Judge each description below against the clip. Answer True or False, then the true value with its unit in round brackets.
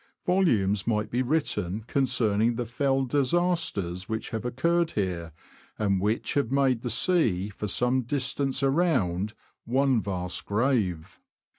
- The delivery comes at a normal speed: False (130 wpm)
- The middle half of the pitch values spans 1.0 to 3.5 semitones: False (5.2 semitones)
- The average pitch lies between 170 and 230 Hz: False (120 Hz)